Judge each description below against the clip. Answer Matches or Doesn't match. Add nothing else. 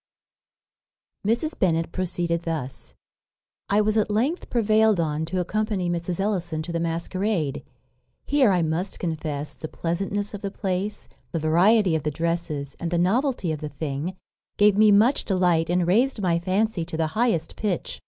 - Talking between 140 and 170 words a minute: Matches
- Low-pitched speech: Doesn't match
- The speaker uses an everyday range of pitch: Matches